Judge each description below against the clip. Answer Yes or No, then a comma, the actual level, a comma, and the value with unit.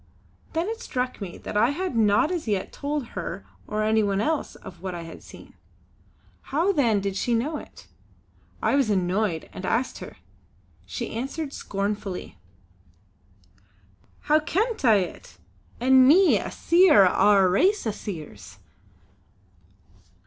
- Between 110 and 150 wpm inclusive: Yes, average, 145 wpm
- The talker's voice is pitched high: Yes, high, 230 Hz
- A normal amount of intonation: No, wide, 7.1 semitones